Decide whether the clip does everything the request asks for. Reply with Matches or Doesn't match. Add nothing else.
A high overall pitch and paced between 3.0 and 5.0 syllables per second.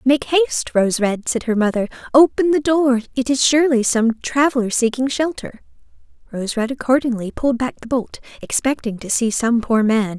Doesn't match